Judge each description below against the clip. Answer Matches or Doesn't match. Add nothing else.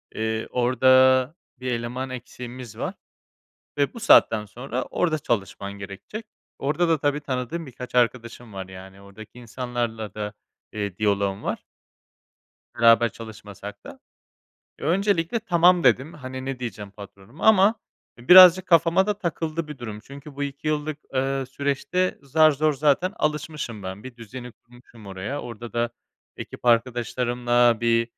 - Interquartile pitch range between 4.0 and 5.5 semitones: Matches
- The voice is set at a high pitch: Doesn't match